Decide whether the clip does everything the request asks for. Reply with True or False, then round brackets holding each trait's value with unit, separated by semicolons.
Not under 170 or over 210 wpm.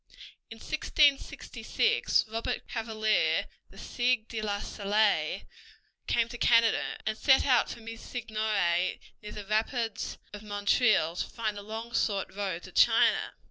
False (140 wpm)